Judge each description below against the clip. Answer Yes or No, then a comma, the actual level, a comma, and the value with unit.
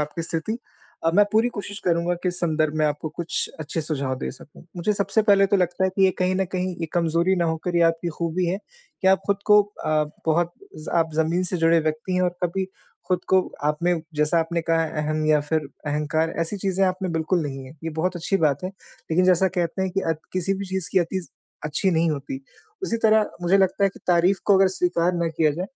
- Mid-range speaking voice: Yes, medium, 175 Hz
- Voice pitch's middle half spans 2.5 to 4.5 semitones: Yes, average, 2.8 semitones